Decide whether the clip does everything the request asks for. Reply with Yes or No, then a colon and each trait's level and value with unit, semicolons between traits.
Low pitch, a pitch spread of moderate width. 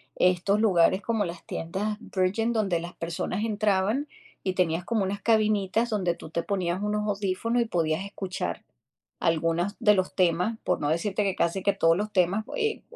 No: high, 195 Hz; average, 3.5 semitones